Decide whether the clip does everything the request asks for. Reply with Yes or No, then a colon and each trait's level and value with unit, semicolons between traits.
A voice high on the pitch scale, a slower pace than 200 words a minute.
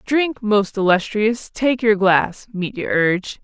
Yes: high, 210 Hz; average, 140 wpm